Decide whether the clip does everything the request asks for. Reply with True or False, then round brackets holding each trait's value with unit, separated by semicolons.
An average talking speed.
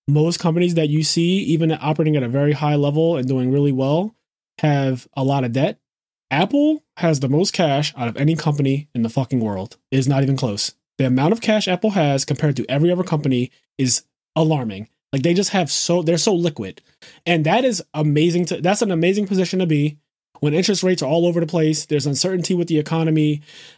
False (210 wpm)